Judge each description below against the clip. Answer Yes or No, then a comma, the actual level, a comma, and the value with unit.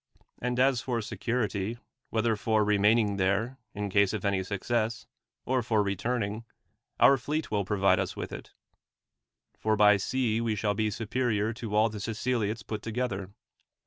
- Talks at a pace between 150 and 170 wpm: Yes, average, 155 wpm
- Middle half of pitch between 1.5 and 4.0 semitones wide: Yes, narrow, 2.6 semitones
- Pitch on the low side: Yes, low, 110 Hz